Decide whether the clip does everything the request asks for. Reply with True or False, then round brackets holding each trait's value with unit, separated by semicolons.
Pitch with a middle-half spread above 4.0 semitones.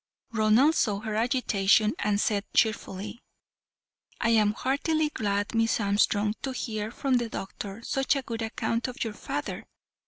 False (2.9 semitones)